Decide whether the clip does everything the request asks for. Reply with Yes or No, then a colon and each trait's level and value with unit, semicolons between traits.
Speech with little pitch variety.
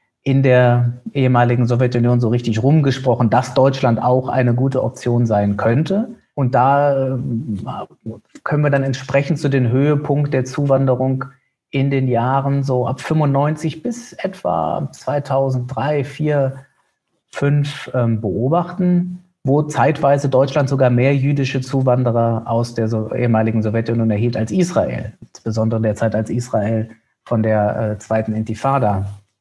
No: average, 3.2 semitones